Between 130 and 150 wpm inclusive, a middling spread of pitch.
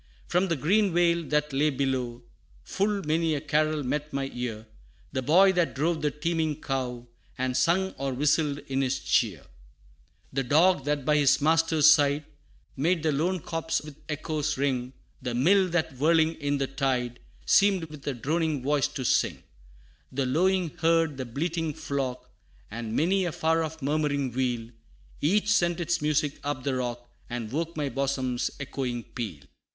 No: average, 165 wpm; average, 3.7 semitones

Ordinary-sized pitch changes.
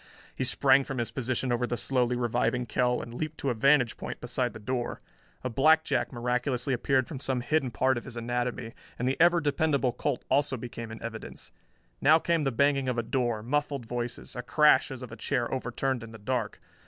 No: narrow, 2.3 semitones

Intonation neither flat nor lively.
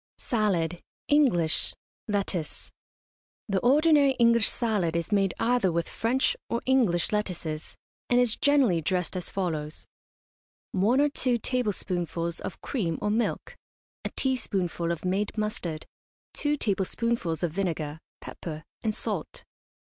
No: wide, 5.8 semitones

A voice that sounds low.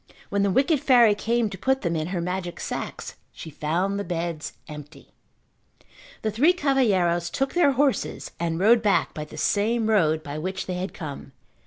No: high, 190 Hz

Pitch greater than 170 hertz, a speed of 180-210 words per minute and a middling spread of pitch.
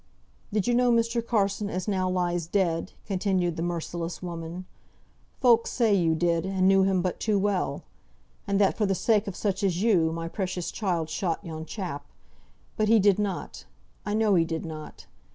Yes: high, 190 Hz; average, 185 wpm; average, 3.3 semitones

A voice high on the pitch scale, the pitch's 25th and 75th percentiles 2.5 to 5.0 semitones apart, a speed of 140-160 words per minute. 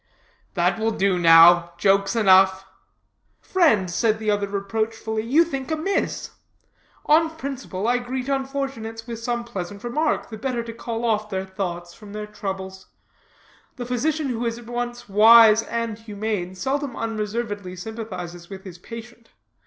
Yes: high, 225 Hz; average, 3.6 semitones; average, 145 wpm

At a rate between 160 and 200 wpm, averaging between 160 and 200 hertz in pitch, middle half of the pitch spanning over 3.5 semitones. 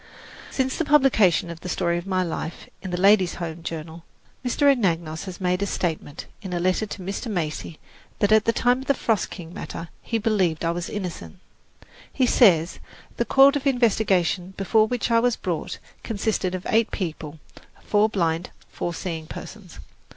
Yes: average, 180 wpm; medium, 185 Hz; average, 4.5 semitones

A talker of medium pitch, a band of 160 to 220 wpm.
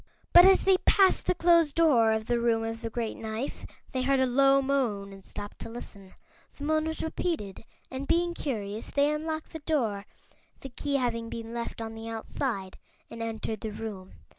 No: high, 240 Hz; average, 190 wpm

